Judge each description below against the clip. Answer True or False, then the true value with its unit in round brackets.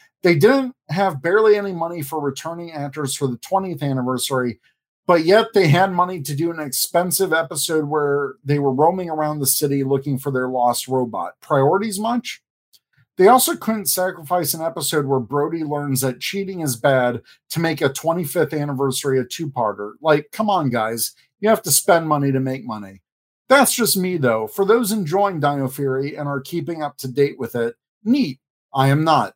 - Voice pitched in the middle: True (150 Hz)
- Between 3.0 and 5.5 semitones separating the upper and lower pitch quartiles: True (5.2 semitones)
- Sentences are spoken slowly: False (185 wpm)